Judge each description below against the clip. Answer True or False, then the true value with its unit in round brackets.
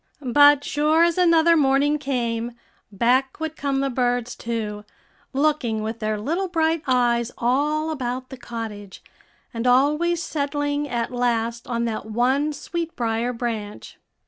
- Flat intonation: False (4.2 semitones)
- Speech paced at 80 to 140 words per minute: True (135 wpm)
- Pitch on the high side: True (255 Hz)